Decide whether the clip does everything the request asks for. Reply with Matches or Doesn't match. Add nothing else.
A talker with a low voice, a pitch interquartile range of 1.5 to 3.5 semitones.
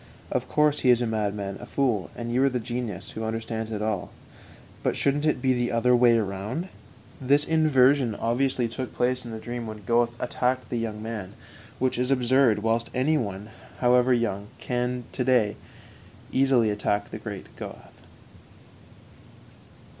Matches